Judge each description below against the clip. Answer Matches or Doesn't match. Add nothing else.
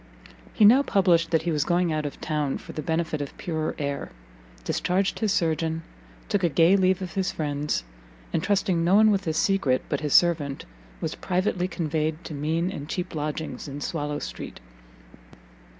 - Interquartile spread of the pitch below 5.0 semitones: Matches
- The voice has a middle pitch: Matches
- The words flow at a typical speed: Matches